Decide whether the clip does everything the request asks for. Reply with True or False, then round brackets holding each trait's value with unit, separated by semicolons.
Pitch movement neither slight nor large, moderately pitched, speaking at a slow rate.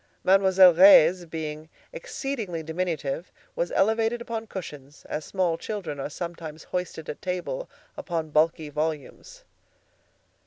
True (4.0 semitones; 175 Hz; 115 wpm)